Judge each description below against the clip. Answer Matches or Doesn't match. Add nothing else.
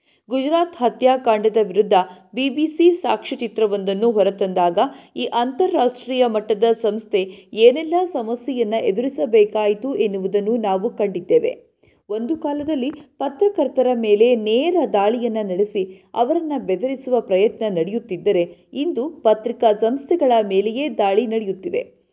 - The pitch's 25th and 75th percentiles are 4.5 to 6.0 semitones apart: Matches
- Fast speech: Doesn't match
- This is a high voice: Matches